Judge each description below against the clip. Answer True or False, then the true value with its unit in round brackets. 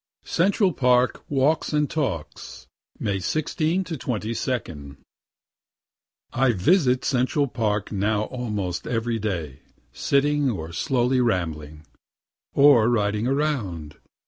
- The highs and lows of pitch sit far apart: True (6.2 semitones)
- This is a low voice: True (120 Hz)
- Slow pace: True (100 wpm)